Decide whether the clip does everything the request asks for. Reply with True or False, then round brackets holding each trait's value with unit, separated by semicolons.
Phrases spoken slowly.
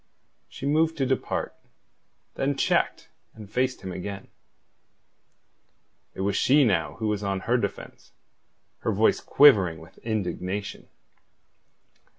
True (120 wpm)